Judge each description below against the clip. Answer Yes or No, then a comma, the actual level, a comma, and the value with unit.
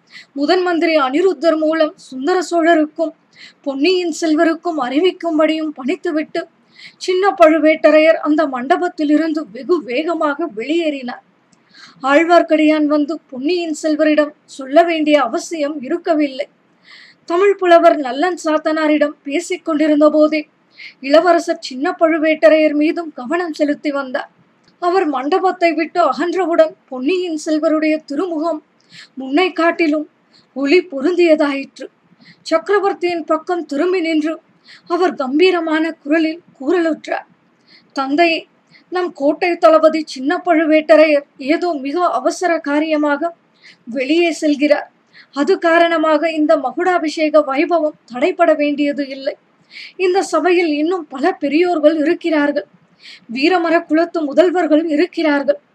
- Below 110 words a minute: Yes, average, 95 wpm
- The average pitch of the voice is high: Yes, very high, 320 Hz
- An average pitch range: No, narrow, 2.1 semitones